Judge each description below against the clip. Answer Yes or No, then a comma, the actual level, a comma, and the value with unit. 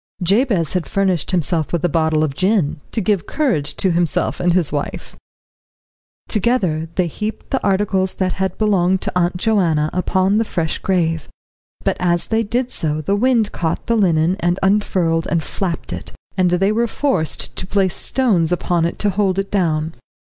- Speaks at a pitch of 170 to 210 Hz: Yes, medium, 185 Hz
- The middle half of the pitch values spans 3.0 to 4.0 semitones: Yes, average, 3.7 semitones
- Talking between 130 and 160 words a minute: No, average, 175 wpm